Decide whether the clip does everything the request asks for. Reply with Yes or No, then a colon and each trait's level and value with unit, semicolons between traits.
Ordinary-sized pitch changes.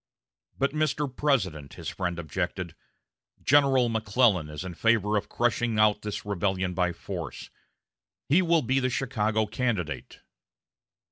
No: wide, 5.8 semitones